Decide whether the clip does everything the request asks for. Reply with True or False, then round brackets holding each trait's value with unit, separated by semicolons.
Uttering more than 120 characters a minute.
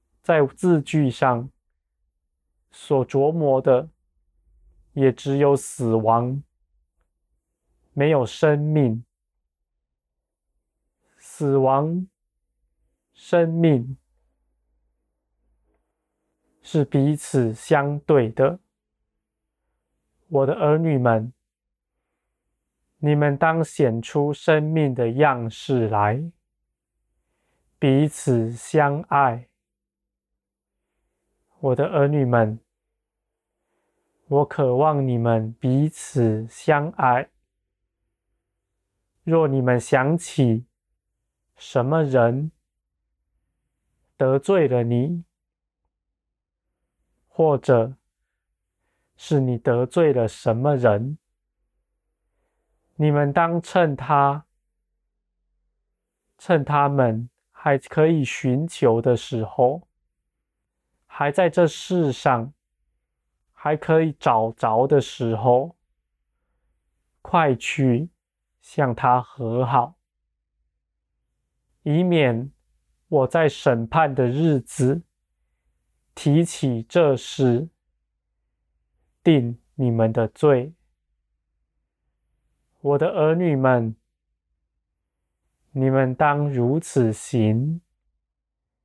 False (100 characters per minute)